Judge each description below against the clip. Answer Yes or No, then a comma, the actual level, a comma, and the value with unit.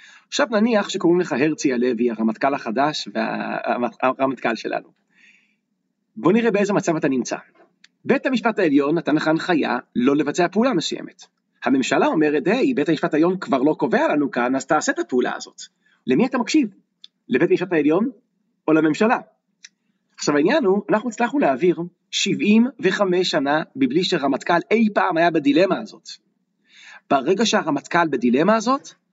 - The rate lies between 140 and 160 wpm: Yes, average, 145 wpm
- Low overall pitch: No, high, 190 Hz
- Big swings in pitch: Yes, wide, 6.0 semitones